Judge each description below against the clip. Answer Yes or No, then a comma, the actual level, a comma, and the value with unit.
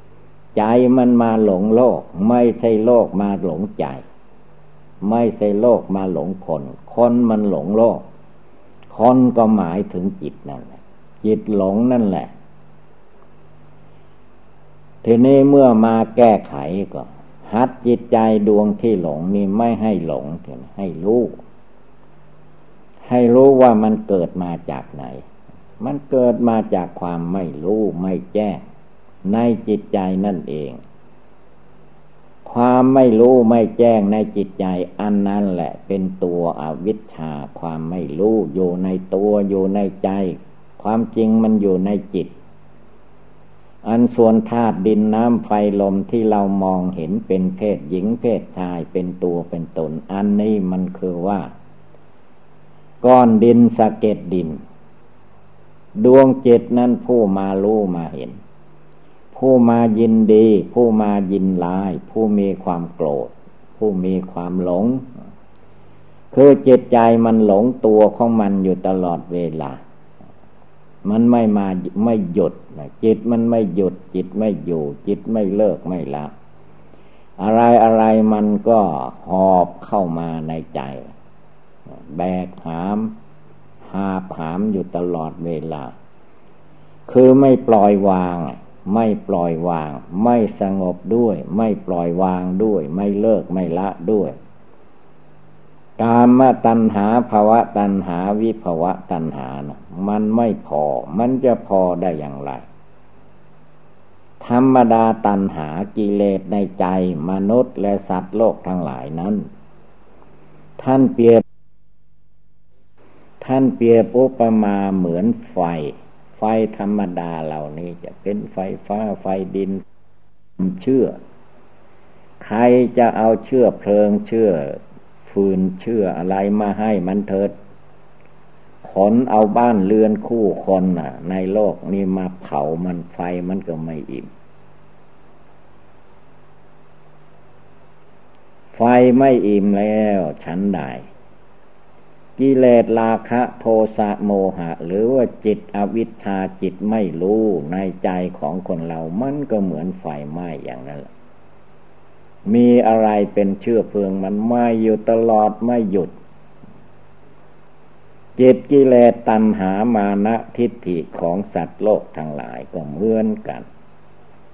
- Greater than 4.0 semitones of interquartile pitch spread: No, average, 3.7 semitones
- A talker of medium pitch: No, low, 100 Hz